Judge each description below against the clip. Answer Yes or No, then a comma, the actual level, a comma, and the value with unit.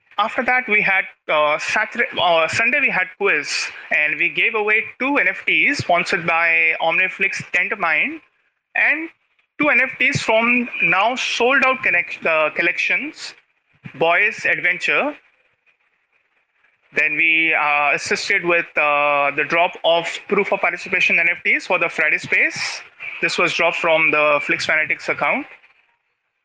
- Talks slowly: Yes, slow, 130 wpm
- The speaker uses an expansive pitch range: Yes, wide, 5.8 semitones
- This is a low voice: No, medium, 185 Hz